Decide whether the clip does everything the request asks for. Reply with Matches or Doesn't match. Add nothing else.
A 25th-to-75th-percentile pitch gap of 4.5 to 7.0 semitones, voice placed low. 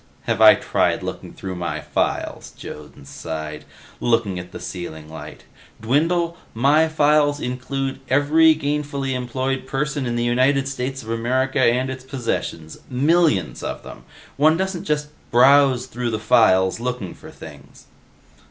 Doesn't match